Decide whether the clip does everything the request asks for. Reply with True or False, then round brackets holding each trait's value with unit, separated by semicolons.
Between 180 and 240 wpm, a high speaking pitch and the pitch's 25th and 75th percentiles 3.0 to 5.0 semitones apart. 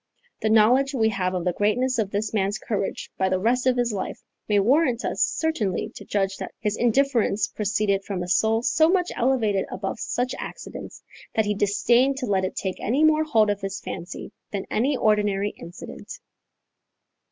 True (185 wpm; 215 Hz; 4.1 semitones)